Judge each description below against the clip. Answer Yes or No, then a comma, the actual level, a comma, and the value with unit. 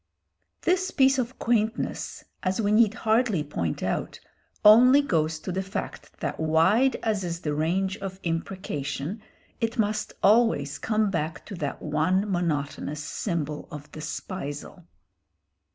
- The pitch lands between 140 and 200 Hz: Yes, high, 190 Hz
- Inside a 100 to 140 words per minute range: Yes, slow, 135 wpm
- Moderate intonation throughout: No, wide, 5.9 semitones